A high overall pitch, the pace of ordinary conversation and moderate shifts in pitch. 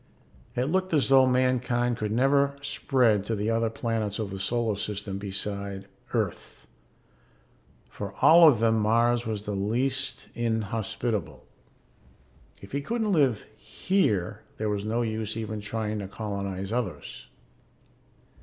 No: low, 110 Hz; average, 145 wpm; average, 3.5 semitones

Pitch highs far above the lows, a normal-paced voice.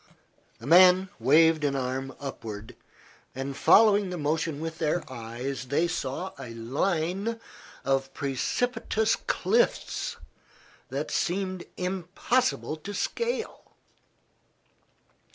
No: wide, 5.9 semitones; slow, 100 wpm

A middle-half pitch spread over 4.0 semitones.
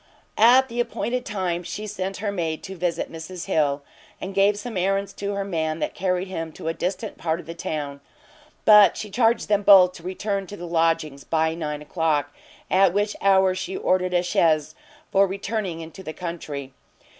No: average, 3.4 semitones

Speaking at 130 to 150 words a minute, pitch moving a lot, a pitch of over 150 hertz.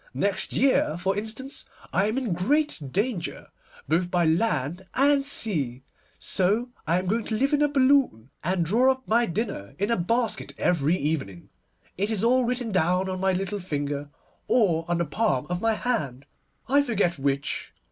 No: average, 175 wpm; wide, 6.5 semitones; high, 190 Hz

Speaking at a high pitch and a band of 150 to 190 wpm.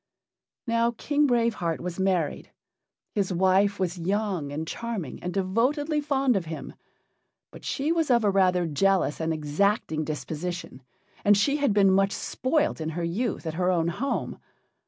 Yes: high, 195 Hz; average, 160 wpm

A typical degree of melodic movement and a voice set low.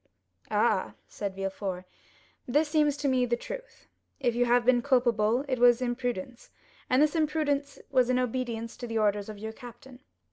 No: average, 3.2 semitones; high, 245 Hz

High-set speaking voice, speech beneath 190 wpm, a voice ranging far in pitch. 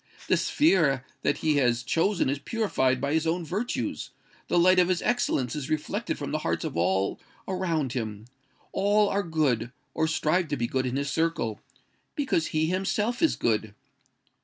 No: medium, 155 Hz; average, 170 wpm; wide, 6.2 semitones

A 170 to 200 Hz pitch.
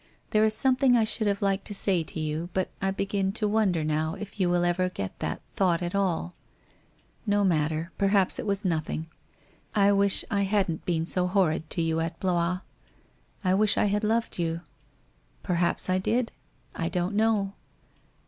Yes: high, 190 Hz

